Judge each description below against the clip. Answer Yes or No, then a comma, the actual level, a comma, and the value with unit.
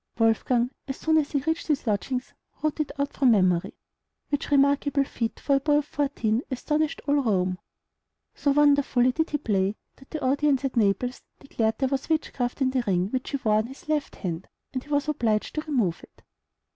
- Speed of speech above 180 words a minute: Yes, average, 195 wpm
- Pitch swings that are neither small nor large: Yes, average, 4.4 semitones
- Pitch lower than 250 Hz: No, very high, 270 Hz